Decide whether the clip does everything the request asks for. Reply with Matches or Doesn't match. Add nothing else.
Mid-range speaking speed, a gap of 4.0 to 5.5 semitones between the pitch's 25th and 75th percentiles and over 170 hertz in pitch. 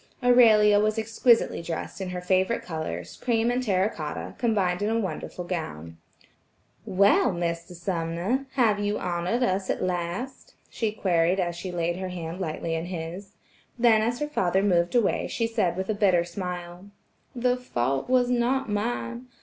Matches